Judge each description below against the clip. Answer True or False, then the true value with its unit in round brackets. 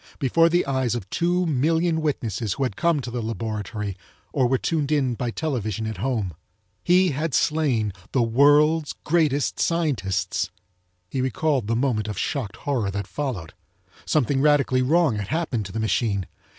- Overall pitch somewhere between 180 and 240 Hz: False (130 Hz)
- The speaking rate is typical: True (165 wpm)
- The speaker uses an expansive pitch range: True (5.8 semitones)